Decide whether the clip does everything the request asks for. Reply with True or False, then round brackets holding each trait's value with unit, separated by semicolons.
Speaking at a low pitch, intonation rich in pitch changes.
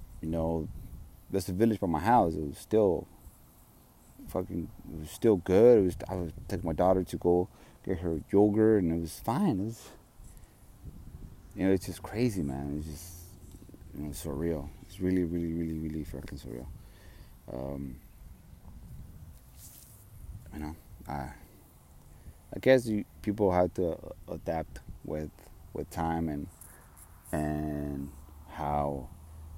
False (85 Hz; 3.9 semitones)